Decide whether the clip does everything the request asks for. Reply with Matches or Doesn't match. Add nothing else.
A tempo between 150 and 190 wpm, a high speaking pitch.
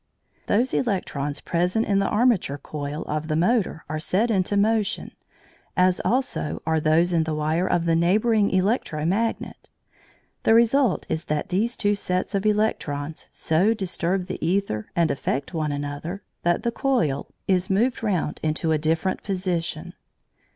Doesn't match